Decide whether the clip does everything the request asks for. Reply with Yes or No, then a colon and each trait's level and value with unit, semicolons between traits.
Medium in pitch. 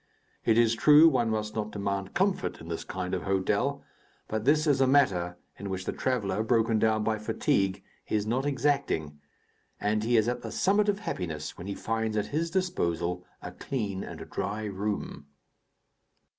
No: low, 110 Hz